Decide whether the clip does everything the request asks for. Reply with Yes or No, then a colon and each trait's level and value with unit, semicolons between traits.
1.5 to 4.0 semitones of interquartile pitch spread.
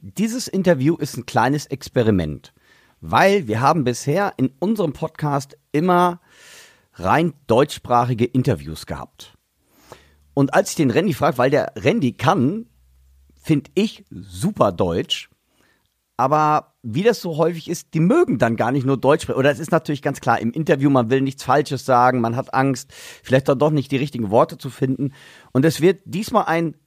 No: average, 4.9 semitones